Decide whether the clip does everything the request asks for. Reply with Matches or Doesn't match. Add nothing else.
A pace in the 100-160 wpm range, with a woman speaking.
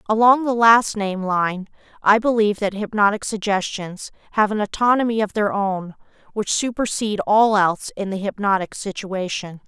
Matches